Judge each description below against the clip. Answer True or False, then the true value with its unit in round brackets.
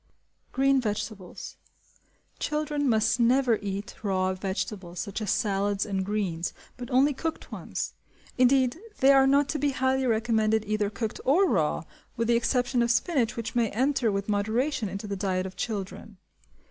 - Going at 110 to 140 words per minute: False (160 wpm)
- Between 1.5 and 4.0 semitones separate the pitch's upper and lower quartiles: False (4.5 semitones)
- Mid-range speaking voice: False (225 Hz)